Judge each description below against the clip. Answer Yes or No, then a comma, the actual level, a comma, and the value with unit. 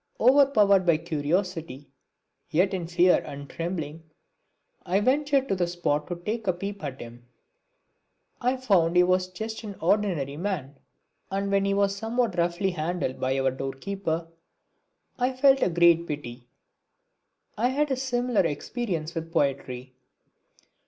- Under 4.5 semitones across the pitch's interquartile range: No, average, 4.9 semitones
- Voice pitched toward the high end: No, medium, 180 Hz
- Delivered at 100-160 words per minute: Yes, average, 145 wpm